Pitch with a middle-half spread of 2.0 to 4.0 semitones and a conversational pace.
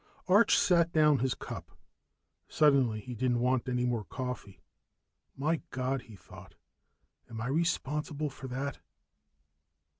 No: average, 3.6 semitones; slow, 125 wpm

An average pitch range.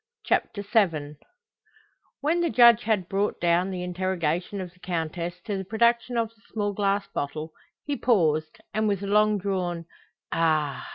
Yes: average, 4.0 semitones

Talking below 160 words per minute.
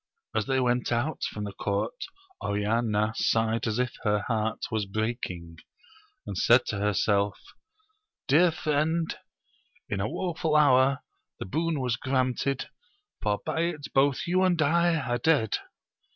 Yes: average, 145 wpm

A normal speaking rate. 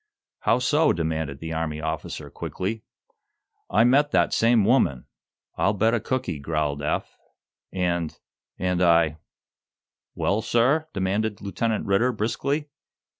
No: slow, 125 wpm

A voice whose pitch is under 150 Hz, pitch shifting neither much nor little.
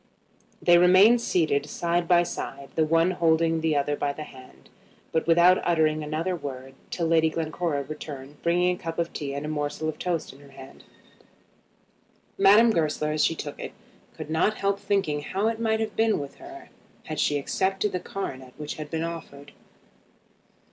No: medium, 160 Hz; average, 3.4 semitones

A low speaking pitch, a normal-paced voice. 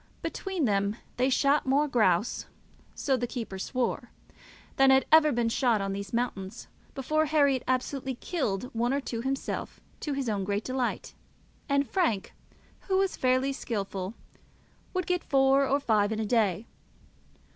No: very high, 255 Hz; average, 155 wpm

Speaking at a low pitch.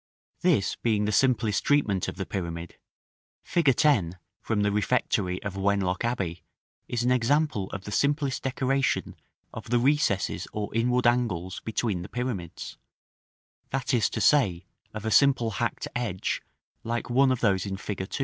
Yes: low, 110 Hz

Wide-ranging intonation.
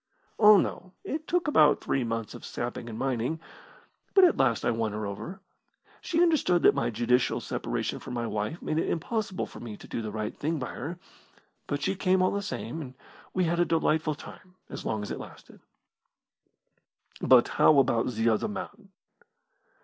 Yes: wide, 8.0 semitones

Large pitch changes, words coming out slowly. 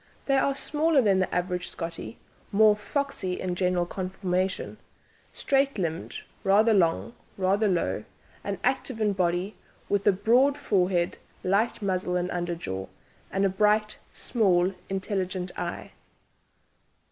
No: average, 3.2 semitones; slow, 125 wpm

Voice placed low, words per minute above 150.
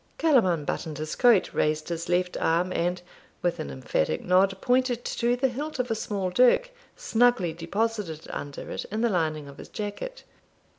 No: high, 190 Hz; average, 170 wpm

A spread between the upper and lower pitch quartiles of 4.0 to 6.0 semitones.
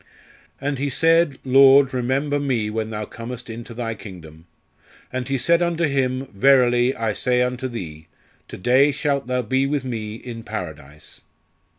No: average, 3.5 semitones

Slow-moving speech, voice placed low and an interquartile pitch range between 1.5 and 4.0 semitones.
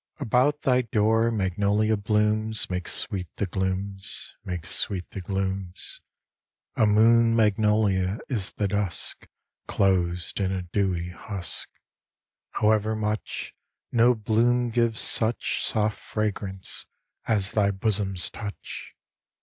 Yes: slow, 110 wpm; low, 105 Hz; narrow, 2.5 semitones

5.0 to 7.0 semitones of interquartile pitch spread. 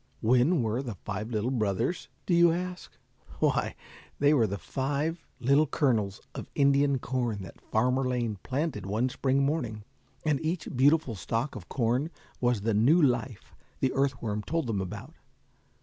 No: average, 4.6 semitones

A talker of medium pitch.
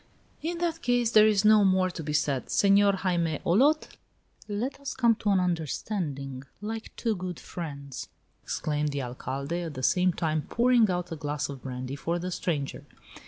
Yes: medium, 180 Hz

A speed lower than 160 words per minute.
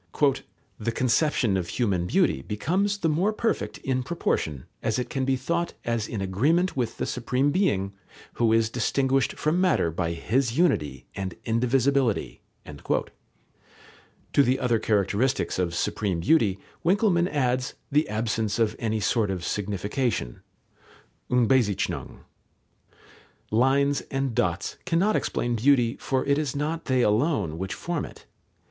Yes: slow, 135 wpm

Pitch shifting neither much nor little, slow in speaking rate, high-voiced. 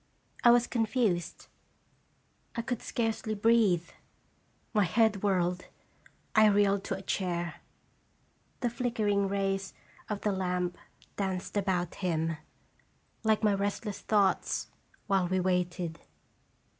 Yes: average, 3.1 semitones; slow, 110 wpm; high, 195 Hz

